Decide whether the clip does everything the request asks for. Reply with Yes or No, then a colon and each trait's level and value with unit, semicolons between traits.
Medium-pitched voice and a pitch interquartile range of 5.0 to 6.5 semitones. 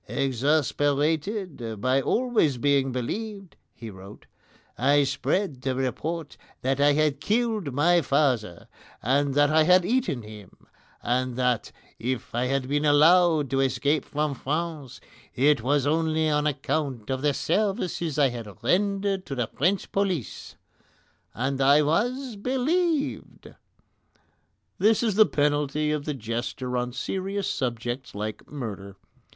Yes: medium, 145 Hz; wide, 5.4 semitones